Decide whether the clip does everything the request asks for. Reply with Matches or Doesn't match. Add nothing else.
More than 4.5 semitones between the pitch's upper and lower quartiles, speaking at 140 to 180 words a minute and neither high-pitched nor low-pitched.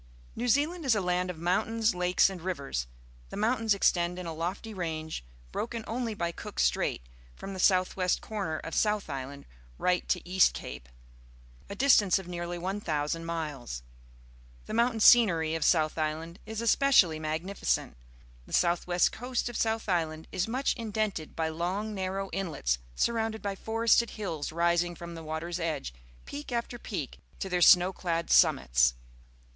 Matches